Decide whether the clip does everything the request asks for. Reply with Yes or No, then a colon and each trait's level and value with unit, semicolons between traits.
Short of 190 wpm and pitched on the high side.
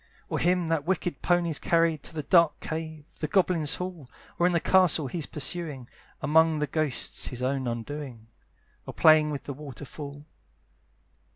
No: average, 160 wpm; medium, 155 Hz